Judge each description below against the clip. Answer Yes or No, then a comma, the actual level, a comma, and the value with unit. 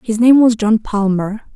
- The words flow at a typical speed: Yes, average, 195 wpm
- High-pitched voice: Yes, high, 220 Hz